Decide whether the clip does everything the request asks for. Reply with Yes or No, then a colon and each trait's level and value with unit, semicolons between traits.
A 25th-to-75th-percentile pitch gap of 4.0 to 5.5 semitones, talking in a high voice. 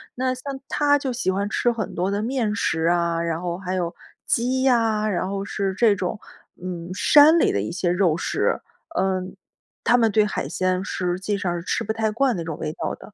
Yes: average, 4.7 semitones; high, 200 Hz